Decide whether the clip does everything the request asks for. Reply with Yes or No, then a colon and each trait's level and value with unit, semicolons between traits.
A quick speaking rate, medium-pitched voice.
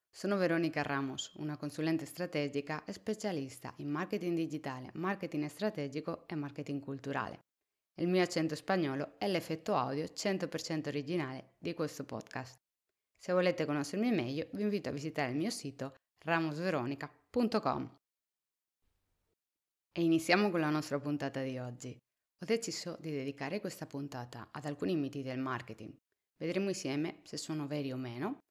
No: average, 140 wpm; medium, 150 Hz